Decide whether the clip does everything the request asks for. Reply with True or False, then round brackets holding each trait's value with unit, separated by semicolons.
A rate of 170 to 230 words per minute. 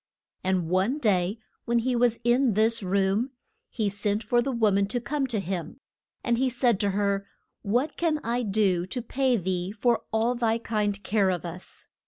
True (190 wpm)